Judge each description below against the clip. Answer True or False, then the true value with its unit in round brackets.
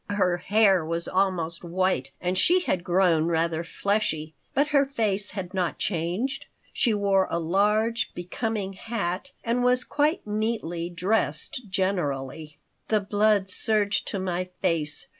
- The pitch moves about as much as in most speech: True (4.0 semitones)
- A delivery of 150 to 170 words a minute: False (140 wpm)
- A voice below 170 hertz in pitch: False (190 Hz)